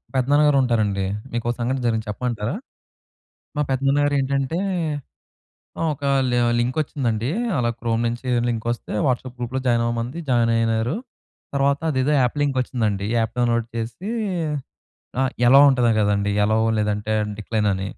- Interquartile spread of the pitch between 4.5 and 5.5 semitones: No, average, 2.8 semitones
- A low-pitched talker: Yes, low, 120 Hz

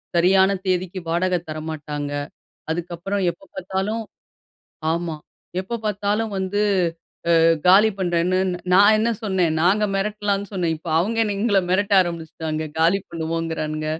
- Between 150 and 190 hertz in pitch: Yes, medium, 185 Hz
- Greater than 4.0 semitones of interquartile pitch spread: No, average, 3.4 semitones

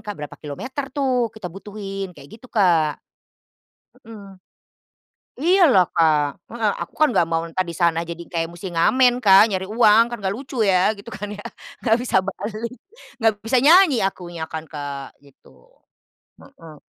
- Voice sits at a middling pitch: No, high, 195 Hz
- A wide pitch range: Yes, wide, 5.7 semitones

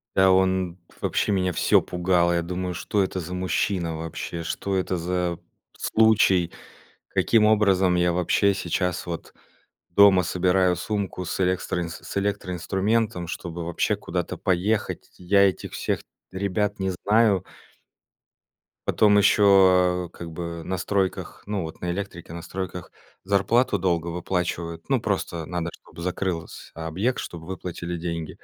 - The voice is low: Yes, very low, 90 Hz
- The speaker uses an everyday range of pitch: No, narrow, 2.2 semitones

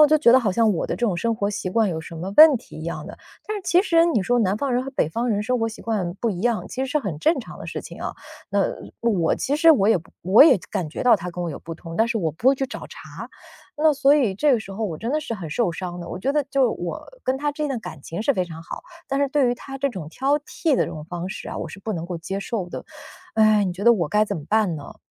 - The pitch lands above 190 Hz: Yes, high, 220 Hz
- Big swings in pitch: Yes, wide, 7.0 semitones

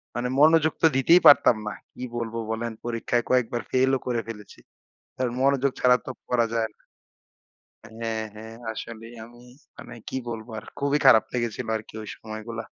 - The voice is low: Yes, low, 120 Hz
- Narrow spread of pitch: Yes, narrow, 2.3 semitones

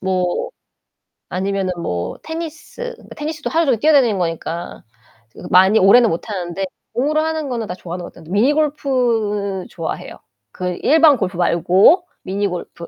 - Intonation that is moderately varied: No, wide, 8.3 semitones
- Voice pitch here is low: No, high, 205 Hz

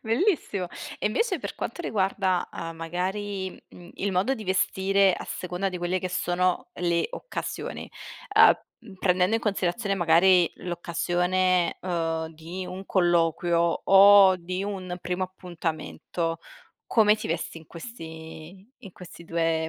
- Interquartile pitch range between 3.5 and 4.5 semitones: No, narrow, 2.4 semitones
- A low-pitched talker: No, medium, 180 Hz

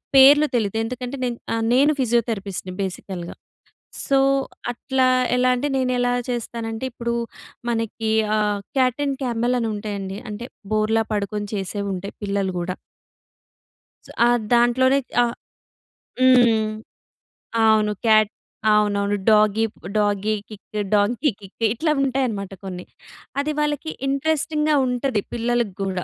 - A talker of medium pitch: No, high, 225 Hz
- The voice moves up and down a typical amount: Yes, average, 3.6 semitones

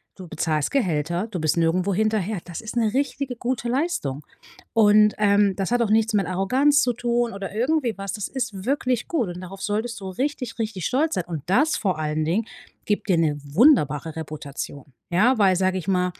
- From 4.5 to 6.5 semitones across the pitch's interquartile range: Yes, wide, 5.4 semitones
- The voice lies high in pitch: Yes, high, 205 Hz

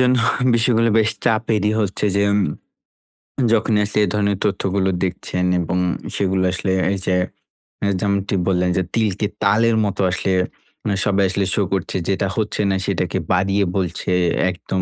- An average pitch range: No, narrow, 2.1 semitones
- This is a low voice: Yes, low, 100 Hz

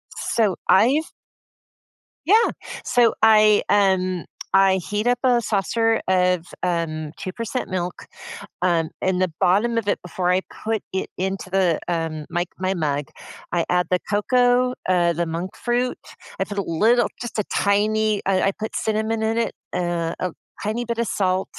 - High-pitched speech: Yes, high, 195 Hz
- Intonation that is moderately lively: Yes, average, 3.9 semitones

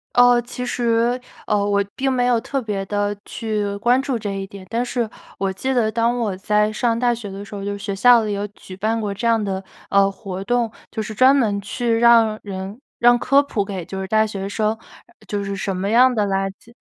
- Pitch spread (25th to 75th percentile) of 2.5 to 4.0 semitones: Yes, average, 3.1 semitones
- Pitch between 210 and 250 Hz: Yes, high, 215 Hz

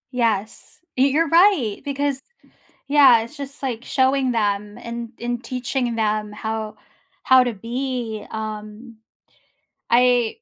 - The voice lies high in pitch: Yes, high, 240 Hz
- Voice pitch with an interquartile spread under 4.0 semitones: Yes, average, 3.3 semitones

